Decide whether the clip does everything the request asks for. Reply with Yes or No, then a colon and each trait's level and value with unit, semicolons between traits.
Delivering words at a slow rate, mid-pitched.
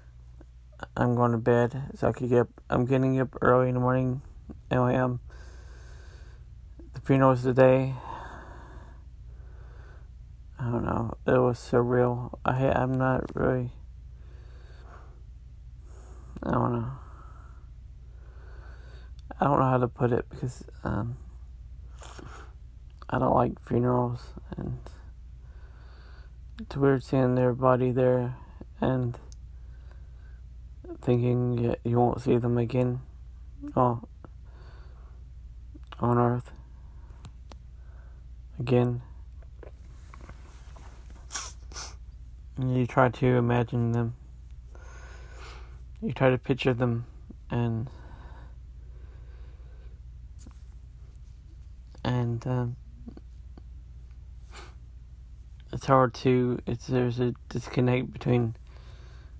No: slow, 90 wpm; very low, 80 Hz